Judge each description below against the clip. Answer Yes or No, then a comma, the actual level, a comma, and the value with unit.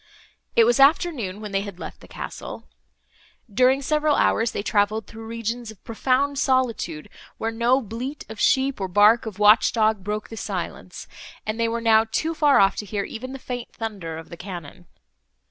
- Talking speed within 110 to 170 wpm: No, average, 185 wpm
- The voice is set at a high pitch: Yes, high, 225 Hz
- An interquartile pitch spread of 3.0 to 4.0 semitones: Yes, average, 3.7 semitones